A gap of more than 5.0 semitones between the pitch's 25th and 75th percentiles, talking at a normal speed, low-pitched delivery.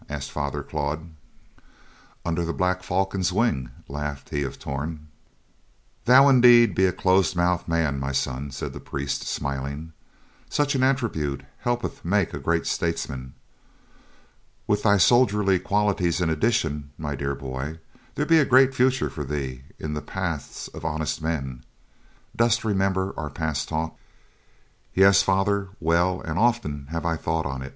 Yes: wide, 5.4 semitones; average, 150 wpm; very low, 85 Hz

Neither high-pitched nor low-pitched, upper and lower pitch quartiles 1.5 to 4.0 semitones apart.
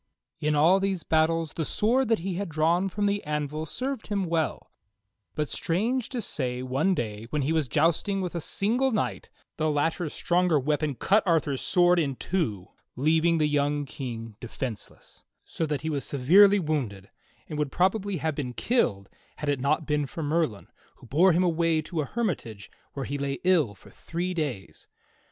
No: medium, 155 Hz; average, 4.4 semitones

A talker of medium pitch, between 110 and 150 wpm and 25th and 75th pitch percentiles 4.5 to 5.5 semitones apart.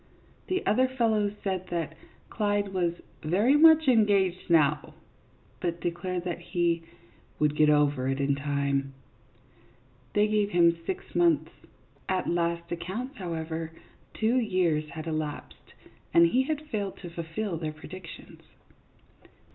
Yes: medium, 175 Hz; average, 140 wpm; average, 5.1 semitones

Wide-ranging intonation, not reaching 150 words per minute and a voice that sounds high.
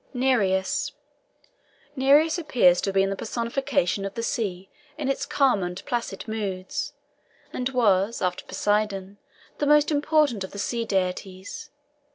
Yes: wide, 5.8 semitones; average, 140 wpm; high, 215 Hz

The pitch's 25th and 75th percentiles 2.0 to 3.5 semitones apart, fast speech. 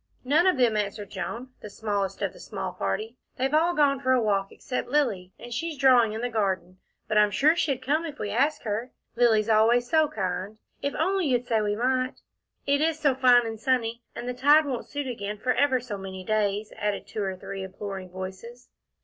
No: average, 4.8 semitones; fast, 210 wpm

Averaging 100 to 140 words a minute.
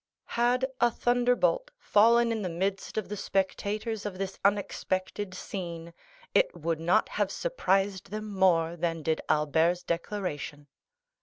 Yes: slow, 135 wpm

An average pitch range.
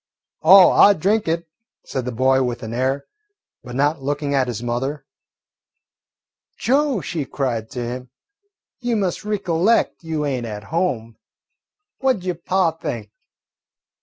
No: wide, 6.6 semitones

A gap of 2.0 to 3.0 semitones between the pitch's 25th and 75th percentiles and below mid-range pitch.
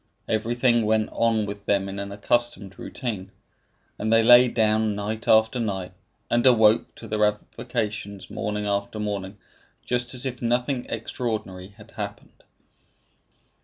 Yes: average, 2.7 semitones; low, 110 Hz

